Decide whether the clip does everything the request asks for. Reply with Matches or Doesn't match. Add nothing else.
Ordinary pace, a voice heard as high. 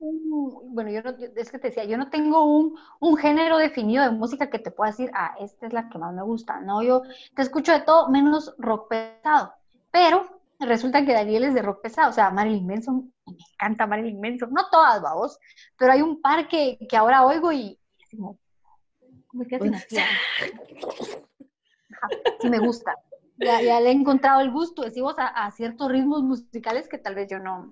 Doesn't match